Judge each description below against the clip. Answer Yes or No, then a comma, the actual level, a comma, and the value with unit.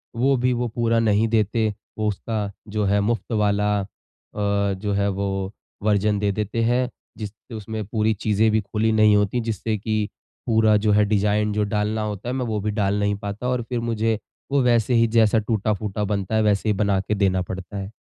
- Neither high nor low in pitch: No, low, 105 Hz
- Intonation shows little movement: Yes, narrow, 1.6 semitones